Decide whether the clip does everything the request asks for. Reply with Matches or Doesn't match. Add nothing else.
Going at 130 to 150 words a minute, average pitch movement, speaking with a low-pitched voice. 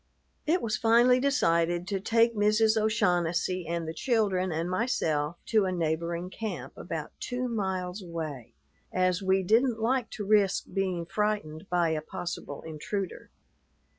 Doesn't match